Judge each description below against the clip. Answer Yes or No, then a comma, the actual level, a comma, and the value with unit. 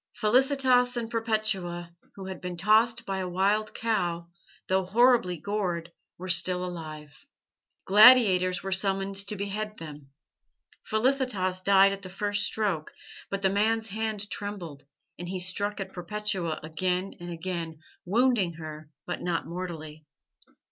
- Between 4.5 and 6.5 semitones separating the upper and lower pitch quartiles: No, average, 3.4 semitones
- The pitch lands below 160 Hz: No, high, 190 Hz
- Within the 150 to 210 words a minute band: No, slow, 135 wpm